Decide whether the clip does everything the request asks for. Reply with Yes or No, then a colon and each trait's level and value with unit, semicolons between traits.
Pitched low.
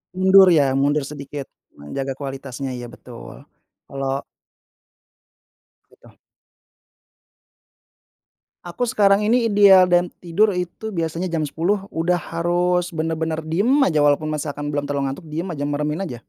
No: medium, 160 Hz